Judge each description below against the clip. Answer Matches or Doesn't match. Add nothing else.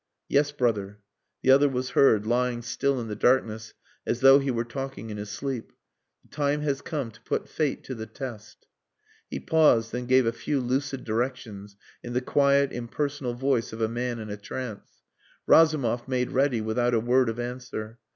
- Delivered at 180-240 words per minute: Matches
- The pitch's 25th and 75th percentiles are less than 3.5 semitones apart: Matches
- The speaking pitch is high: Doesn't match